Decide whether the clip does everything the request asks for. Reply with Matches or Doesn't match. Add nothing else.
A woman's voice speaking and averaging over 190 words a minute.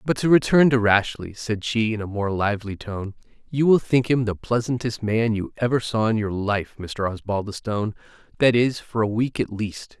Doesn't match